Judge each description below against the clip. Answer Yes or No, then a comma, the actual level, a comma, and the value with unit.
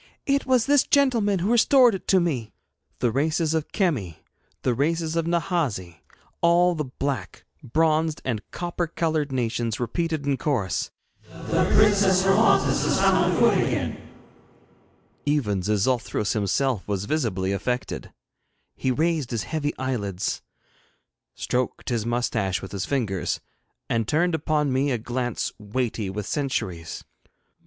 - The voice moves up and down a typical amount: No, wide, 7.1 semitones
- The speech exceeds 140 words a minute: No, slow, 135 wpm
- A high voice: No, low, 135 Hz